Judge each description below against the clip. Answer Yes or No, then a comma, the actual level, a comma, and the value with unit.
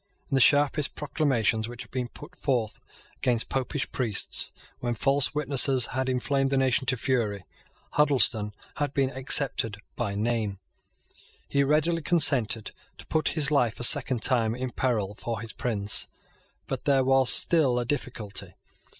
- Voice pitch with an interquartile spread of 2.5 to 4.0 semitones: Yes, average, 3.4 semitones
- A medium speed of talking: Yes, average, 150 wpm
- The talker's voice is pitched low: Yes, low, 130 Hz